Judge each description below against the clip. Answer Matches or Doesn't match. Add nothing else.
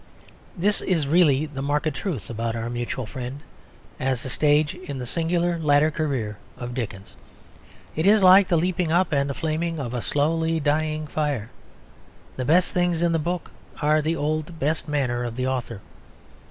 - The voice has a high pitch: Doesn't match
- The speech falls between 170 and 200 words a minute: Matches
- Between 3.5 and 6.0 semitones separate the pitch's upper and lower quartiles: Matches